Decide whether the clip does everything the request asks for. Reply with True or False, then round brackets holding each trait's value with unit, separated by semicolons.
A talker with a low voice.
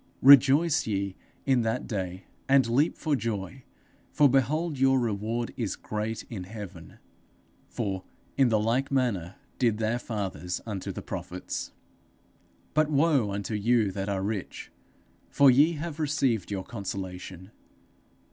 True (115 Hz)